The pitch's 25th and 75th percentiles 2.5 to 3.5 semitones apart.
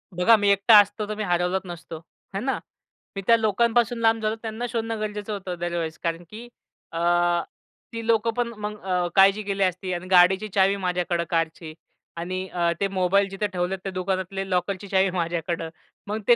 Yes: average, 3.1 semitones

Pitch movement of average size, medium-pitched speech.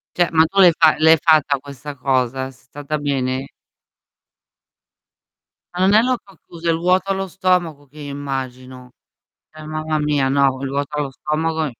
Yes: average, 3.3 semitones; medium, 150 Hz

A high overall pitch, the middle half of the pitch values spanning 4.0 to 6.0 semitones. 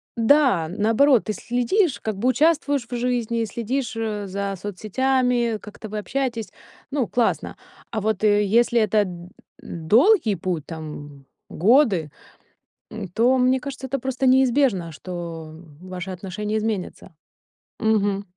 Yes: high, 220 Hz; average, 4.8 semitones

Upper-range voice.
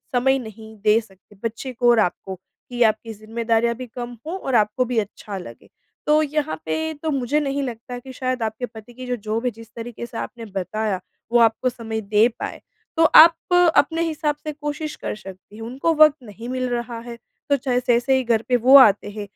Yes: high, 235 Hz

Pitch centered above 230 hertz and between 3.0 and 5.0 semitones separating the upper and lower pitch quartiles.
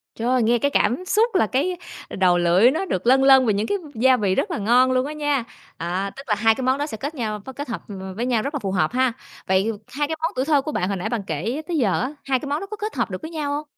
No: very high, 255 Hz; wide, 5.4 semitones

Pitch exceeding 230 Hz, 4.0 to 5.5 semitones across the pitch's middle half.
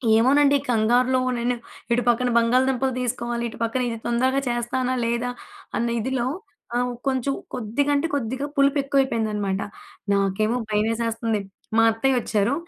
No: high, 240 Hz; narrow, 2.5 semitones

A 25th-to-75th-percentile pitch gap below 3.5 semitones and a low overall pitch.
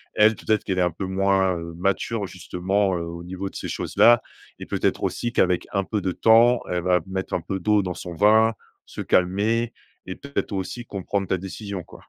Yes: average, 2.8 semitones; very low, 95 Hz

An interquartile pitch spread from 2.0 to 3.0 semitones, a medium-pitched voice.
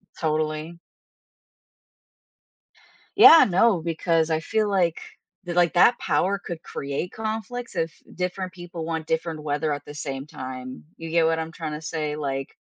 Yes: average, 2.7 semitones; medium, 165 Hz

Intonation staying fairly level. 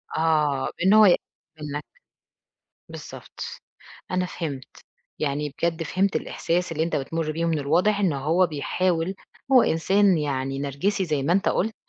No: average, 3.8 semitones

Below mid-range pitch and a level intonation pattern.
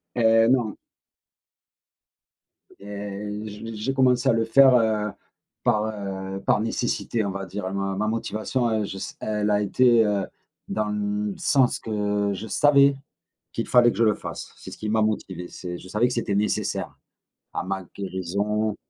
Yes: low, 105 Hz; narrow, 2.2 semitones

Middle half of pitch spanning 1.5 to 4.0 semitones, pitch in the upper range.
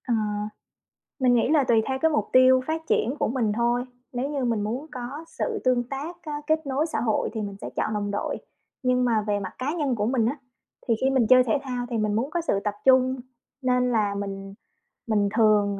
Yes: average, 3.7 semitones; high, 245 Hz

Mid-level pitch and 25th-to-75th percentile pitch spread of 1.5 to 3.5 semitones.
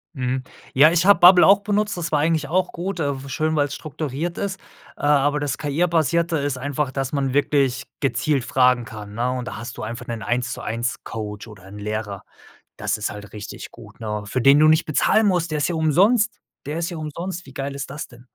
No: medium, 145 Hz; average, 5.1 semitones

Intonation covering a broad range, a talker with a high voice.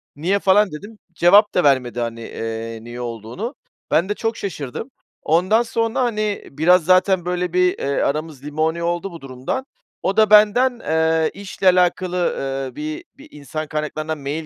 No: wide, 5.7 semitones; medium, 170 Hz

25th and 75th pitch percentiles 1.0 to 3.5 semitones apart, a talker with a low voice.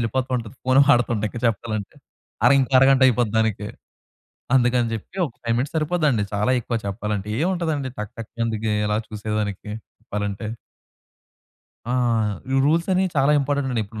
No: average, 4.2 semitones; low, 120 Hz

